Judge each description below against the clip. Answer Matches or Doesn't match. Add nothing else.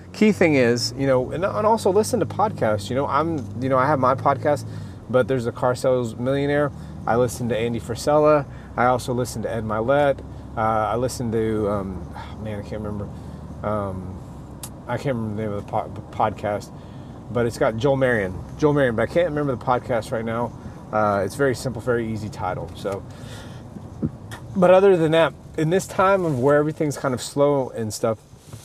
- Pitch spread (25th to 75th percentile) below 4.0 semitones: Doesn't match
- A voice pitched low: Matches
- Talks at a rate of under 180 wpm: Doesn't match